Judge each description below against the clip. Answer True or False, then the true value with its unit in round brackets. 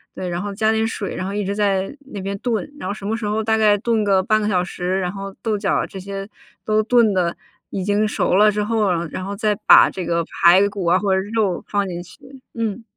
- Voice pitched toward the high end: True (200 Hz)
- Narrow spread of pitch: True (2.3 semitones)